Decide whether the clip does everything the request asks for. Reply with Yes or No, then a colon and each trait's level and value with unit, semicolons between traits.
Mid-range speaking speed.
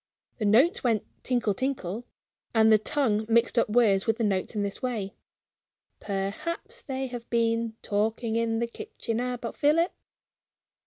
Yes: average, 150 wpm